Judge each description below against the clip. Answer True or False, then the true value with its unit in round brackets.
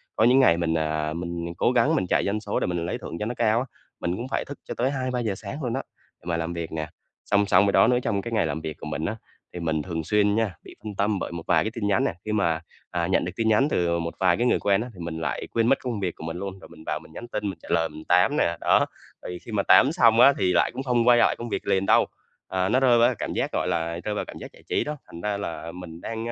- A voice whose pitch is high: False (100 Hz)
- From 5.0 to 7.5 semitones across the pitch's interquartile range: True (5.3 semitones)